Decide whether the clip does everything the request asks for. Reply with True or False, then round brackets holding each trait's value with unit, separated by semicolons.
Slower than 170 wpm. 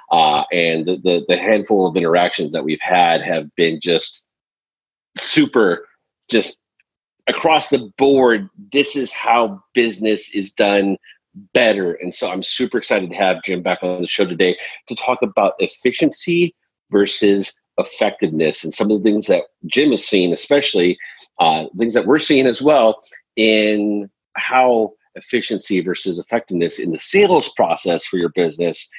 True (155 wpm)